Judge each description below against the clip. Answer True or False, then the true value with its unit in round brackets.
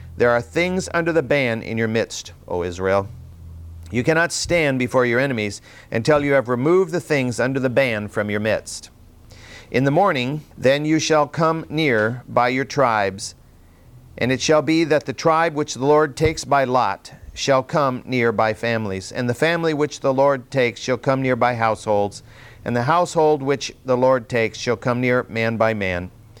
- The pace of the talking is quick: False (190 wpm)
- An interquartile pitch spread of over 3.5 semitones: True (4.8 semitones)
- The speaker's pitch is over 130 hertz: False (125 Hz)